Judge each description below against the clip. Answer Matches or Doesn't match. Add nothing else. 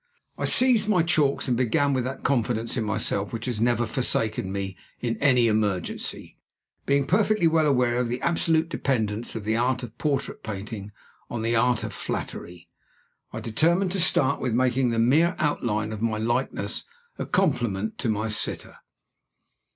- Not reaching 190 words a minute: Matches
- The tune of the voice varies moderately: Matches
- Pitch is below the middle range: Matches